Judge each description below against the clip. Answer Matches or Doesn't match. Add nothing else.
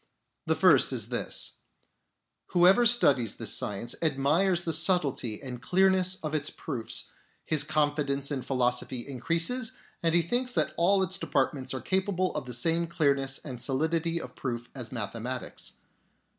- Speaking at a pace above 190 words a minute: Doesn't match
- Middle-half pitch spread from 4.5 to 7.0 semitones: Matches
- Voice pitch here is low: Doesn't match